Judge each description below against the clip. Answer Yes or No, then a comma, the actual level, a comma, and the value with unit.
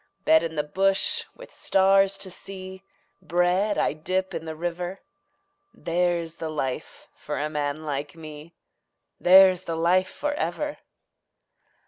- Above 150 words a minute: No, slow, 135 wpm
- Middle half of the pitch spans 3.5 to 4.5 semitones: No, average, 3.1 semitones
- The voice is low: No, medium, 175 Hz